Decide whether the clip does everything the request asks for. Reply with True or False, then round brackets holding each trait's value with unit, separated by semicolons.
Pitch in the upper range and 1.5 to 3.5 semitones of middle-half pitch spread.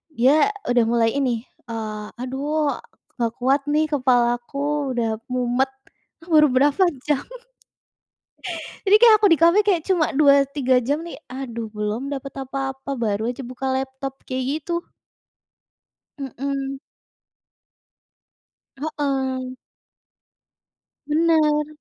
True (270 Hz; 3.2 semitones)